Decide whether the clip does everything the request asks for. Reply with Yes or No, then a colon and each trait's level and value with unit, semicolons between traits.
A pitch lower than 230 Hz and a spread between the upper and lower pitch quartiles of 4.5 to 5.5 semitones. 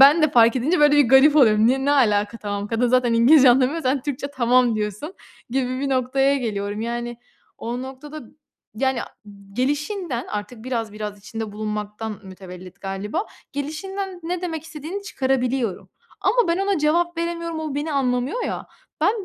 No: very high, 260 Hz; average, 5.2 semitones